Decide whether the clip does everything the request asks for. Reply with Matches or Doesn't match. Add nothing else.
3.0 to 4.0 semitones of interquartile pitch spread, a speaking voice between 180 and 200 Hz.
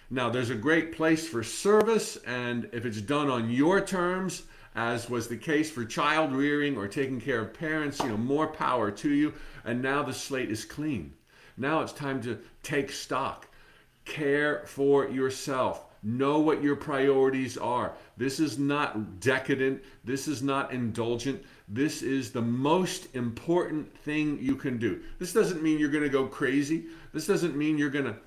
Doesn't match